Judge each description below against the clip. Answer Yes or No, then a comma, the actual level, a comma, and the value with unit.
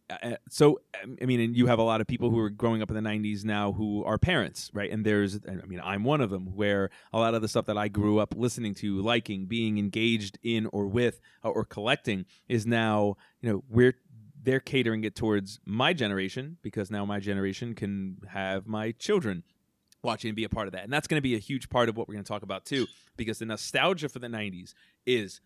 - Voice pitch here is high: No, low, 110 Hz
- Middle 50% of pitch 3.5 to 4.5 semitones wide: No, average, 2.8 semitones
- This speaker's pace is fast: Yes, fast, 240 wpm